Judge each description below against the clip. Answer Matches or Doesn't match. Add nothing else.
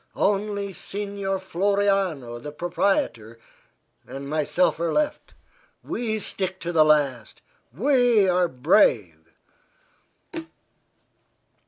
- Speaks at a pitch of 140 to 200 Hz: Matches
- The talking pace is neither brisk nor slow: Doesn't match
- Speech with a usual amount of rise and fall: Matches